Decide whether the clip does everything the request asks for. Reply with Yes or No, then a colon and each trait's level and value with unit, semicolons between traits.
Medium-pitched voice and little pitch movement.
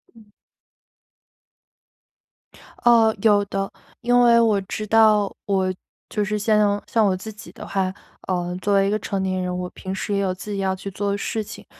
No: high, 200 Hz; narrow, 2.1 semitones